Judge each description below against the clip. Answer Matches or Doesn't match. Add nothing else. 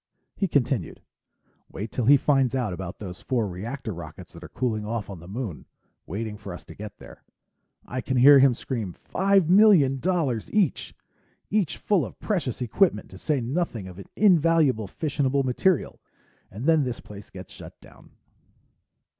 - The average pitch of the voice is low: Matches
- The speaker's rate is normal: Matches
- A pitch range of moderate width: Doesn't match